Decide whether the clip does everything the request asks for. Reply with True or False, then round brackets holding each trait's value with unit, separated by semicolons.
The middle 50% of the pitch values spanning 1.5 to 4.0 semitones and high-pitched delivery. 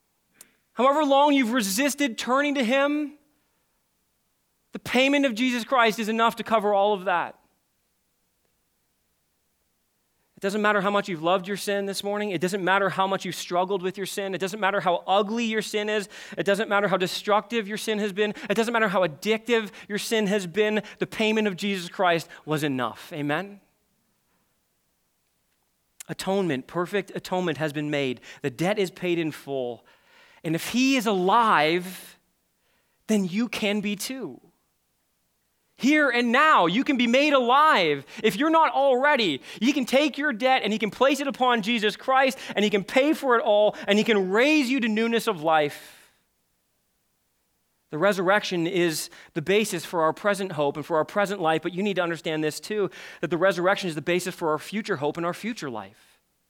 False (4.9 semitones; 200 Hz)